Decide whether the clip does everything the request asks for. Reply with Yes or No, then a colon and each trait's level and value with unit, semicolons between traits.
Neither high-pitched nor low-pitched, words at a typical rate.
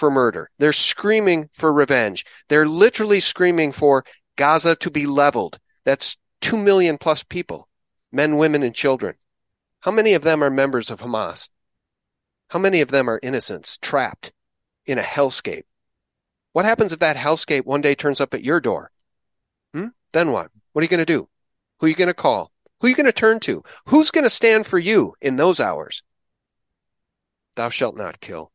Yes: medium, 155 Hz; average, 185 wpm